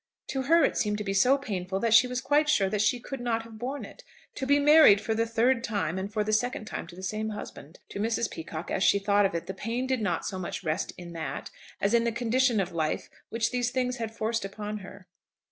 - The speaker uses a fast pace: Yes, fast, 255 wpm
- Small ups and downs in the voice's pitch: No, average, 4.0 semitones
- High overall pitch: Yes, high, 220 Hz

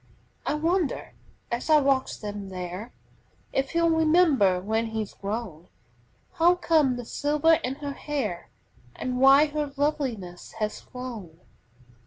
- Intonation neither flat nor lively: No, wide, 6.2 semitones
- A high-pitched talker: Yes, very high, 260 Hz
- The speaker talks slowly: Yes, slow, 130 wpm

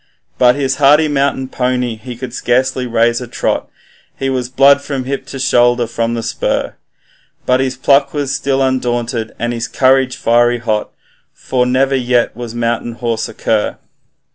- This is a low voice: Yes, low, 125 Hz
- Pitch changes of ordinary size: No, narrow, 2.1 semitones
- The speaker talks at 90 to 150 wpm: No, average, 165 wpm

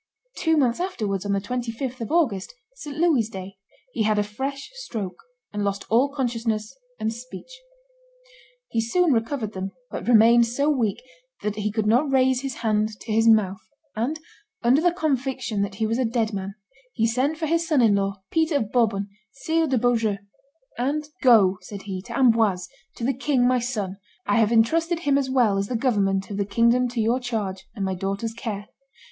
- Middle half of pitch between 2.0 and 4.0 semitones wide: No, average, 4.4 semitones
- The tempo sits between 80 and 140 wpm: No, average, 190 wpm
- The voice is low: No, high, 230 Hz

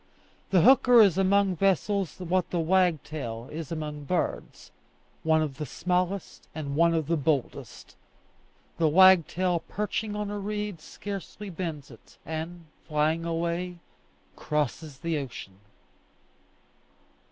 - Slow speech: Yes, slow, 120 wpm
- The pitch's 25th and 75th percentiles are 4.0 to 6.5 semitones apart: No, average, 3.5 semitones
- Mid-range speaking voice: Yes, medium, 170 Hz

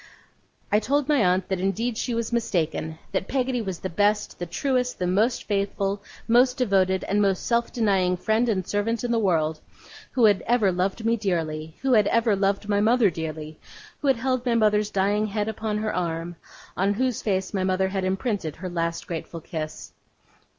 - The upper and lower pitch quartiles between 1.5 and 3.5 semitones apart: No, average, 3.9 semitones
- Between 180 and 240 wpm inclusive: Yes, average, 190 wpm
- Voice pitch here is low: No, high, 205 Hz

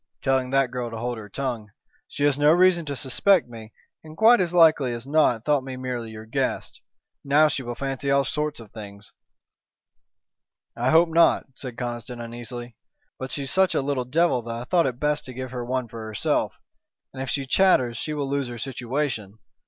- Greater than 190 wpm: Yes, average, 200 wpm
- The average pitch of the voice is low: Yes, low, 130 Hz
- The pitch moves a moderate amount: Yes, average, 3.7 semitones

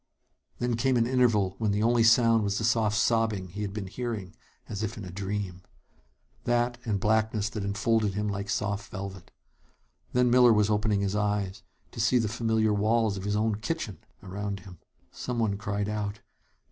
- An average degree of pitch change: No, narrow, 2.3 semitones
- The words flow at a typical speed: Yes, average, 180 wpm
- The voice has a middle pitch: No, low, 105 Hz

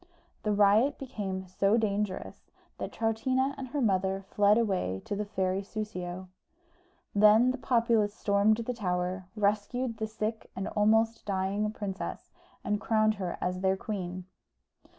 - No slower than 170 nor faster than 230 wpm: No, average, 140 wpm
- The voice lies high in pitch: Yes, high, 210 Hz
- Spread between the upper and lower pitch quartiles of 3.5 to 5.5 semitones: No, average, 2.7 semitones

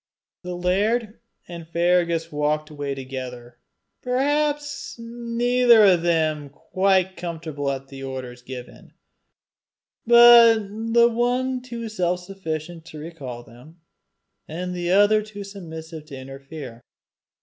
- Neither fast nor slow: No, slow, 115 wpm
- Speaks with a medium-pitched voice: Yes, medium, 175 Hz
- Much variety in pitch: Yes, wide, 7.1 semitones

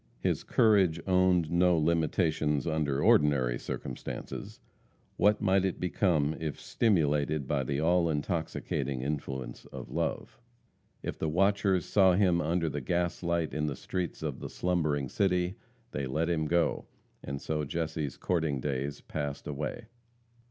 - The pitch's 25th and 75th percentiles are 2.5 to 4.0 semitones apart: Yes, average, 3.6 semitones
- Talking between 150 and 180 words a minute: No, average, 140 wpm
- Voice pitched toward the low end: Yes, very low, 80 Hz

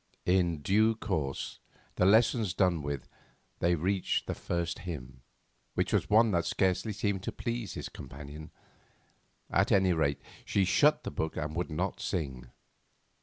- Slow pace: No, average, 150 wpm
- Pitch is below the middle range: Yes, very low, 90 Hz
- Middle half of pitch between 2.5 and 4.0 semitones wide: No, average, 4.6 semitones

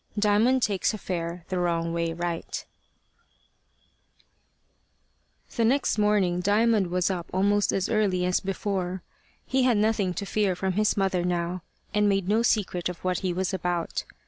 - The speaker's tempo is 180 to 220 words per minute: No, average, 155 wpm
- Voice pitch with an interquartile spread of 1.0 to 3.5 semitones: Yes, average, 2.8 semitones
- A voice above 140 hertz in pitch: Yes, high, 190 Hz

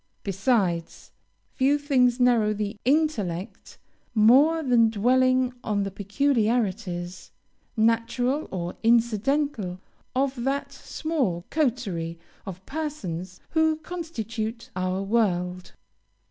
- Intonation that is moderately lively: No, wide, 5.8 semitones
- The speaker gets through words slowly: Yes, slow, 90 wpm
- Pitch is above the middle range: Yes, high, 230 Hz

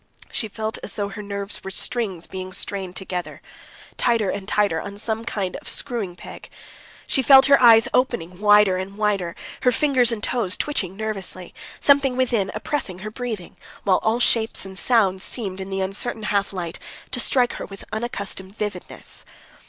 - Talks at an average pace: Yes, average, 170 wpm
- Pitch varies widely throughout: No, average, 3.5 semitones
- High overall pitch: Yes, high, 205 Hz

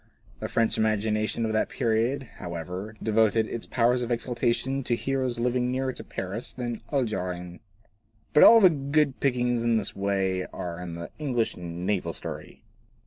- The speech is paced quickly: No, average, 165 wpm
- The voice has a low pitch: Yes, low, 115 Hz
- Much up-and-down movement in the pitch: No, average, 4.2 semitones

